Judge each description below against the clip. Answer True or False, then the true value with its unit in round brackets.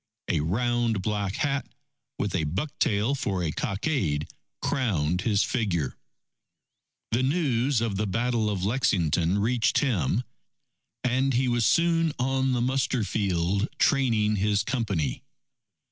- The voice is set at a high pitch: False (110 Hz)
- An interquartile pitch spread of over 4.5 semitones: True (5.1 semitones)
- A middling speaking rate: False (130 wpm)